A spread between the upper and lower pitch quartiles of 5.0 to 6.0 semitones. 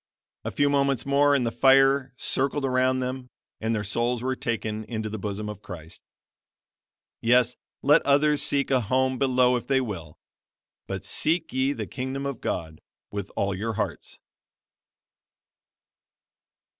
No: average, 3.9 semitones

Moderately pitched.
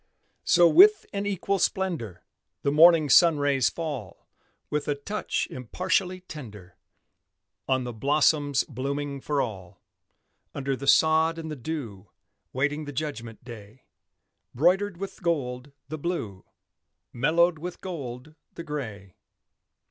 Yes: medium, 145 Hz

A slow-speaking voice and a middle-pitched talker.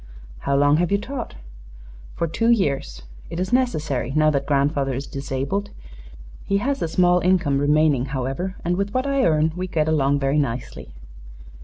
No: average, 170 wpm; medium, 155 Hz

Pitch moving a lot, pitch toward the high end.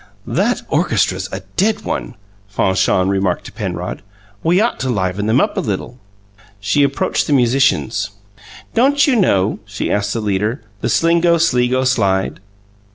No: wide, 8.7 semitones; low, 115 Hz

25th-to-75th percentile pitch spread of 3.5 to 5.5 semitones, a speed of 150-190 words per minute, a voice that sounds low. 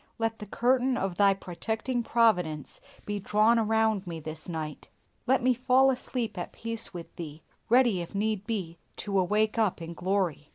No: average, 4.6 semitones; average, 170 wpm; high, 210 Hz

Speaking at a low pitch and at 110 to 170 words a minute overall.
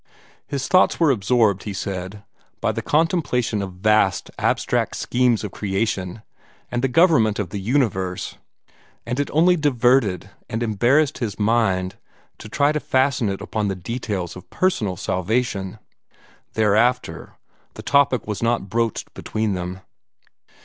Yes: low, 110 Hz; average, 140 wpm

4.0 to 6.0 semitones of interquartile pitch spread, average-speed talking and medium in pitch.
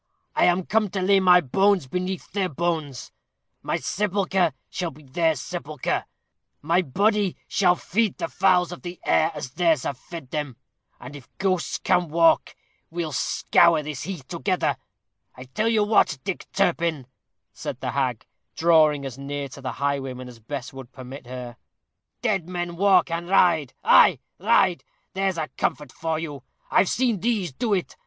Yes: average, 4.9 semitones; average, 165 wpm; medium, 170 Hz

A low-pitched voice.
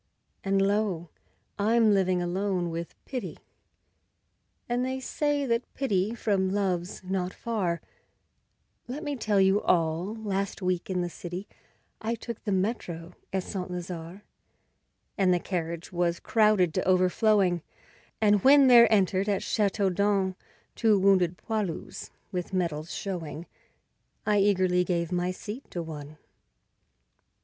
No: high, 190 Hz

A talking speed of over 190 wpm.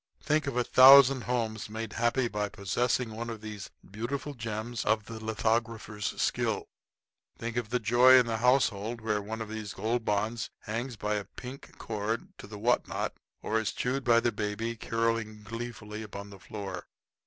No: average, 175 wpm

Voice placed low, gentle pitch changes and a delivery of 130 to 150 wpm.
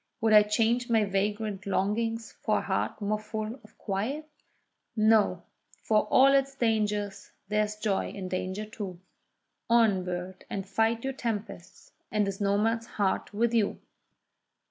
No: high, 215 Hz; narrow, 2.2 semitones; average, 145 wpm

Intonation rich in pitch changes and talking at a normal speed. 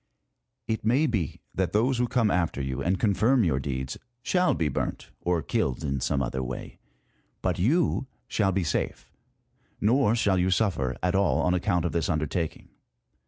Yes: wide, 6.6 semitones; average, 175 wpm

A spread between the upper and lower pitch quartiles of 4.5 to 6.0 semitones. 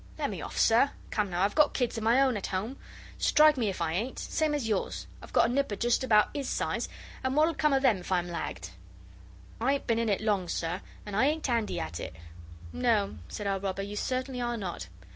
Yes: average, 5.1 semitones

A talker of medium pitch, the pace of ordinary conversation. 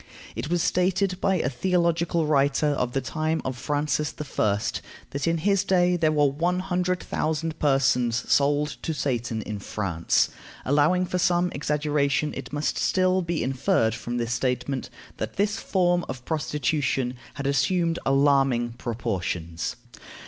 Yes: medium, 150 Hz; average, 145 wpm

